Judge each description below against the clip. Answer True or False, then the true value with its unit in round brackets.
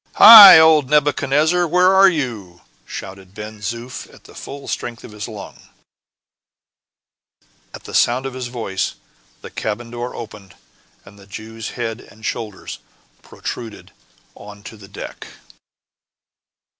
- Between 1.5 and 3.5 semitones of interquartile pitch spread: False (5.3 semitones)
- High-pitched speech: False (115 Hz)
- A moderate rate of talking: False (130 wpm)